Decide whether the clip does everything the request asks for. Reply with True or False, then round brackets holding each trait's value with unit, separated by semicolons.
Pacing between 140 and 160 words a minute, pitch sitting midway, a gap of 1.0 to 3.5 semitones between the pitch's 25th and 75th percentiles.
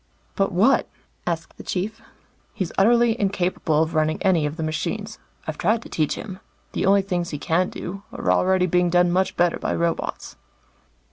False (180 wpm; 180 Hz; 3.1 semitones)